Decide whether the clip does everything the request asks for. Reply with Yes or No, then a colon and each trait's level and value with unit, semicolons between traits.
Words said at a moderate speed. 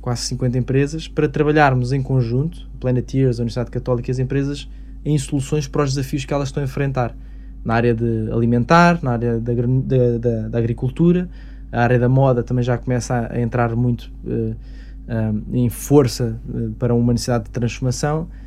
Yes: average, 175 wpm